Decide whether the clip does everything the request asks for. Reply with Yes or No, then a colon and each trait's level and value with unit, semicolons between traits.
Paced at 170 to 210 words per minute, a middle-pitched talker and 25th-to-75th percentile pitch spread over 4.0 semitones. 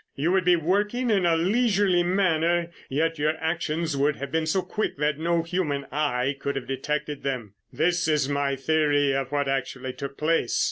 No: average, 185 wpm; medium, 155 Hz; average, 3.7 semitones